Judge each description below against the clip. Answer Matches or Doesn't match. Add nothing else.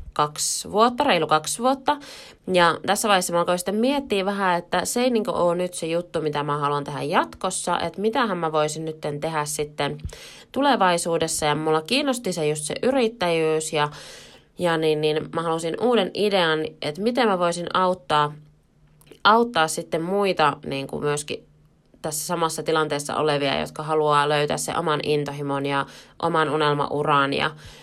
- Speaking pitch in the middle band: Matches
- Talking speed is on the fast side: Matches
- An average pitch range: Matches